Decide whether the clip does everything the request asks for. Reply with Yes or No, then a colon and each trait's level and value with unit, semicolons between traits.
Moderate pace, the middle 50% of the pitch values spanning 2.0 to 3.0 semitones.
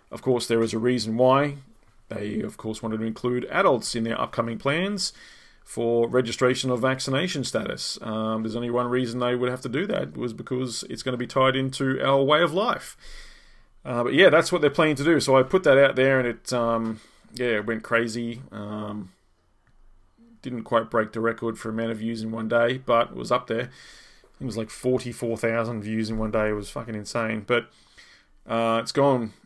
No: fast, 210 wpm; narrow, 2.6 semitones